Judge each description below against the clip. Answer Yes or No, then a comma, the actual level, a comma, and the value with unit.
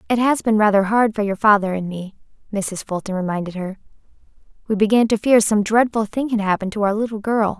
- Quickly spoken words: Yes, fast, 215 wpm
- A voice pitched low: No, high, 210 Hz